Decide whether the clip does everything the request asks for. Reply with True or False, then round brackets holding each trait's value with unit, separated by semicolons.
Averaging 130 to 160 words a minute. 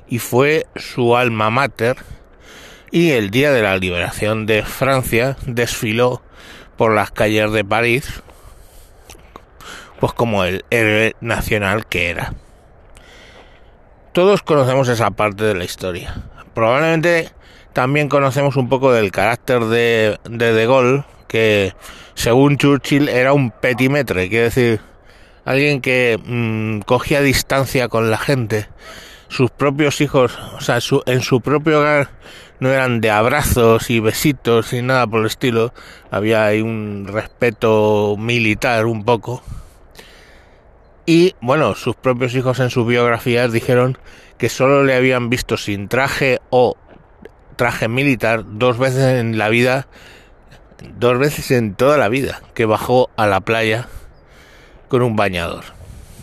True (135 wpm)